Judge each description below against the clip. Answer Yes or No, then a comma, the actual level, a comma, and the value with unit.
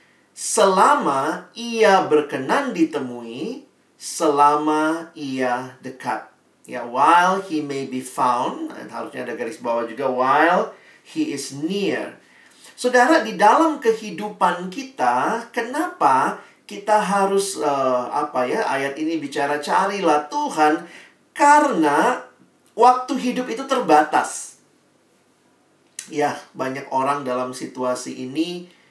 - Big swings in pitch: Yes, wide, 8.6 semitones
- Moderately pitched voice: Yes, medium, 160 Hz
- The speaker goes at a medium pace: Yes, average, 100 wpm